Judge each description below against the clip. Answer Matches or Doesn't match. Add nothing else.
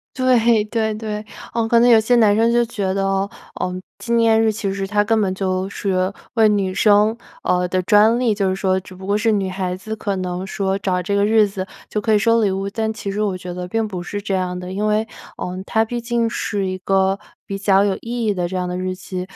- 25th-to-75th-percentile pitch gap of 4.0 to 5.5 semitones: Doesn't match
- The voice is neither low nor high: Doesn't match